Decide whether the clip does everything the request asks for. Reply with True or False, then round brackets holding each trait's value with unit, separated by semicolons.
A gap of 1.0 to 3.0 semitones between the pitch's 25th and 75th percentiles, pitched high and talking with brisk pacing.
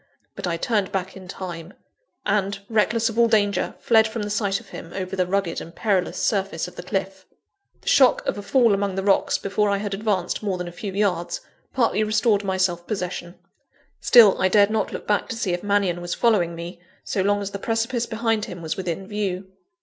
True (2.6 semitones; 200 Hz; 215 wpm)